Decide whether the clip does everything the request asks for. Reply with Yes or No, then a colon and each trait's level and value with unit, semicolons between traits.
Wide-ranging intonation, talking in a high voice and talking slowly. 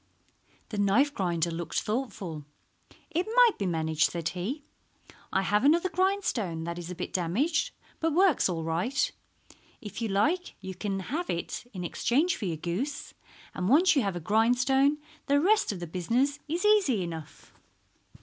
No: wide, 8.9 semitones; high, 210 Hz; average, 165 wpm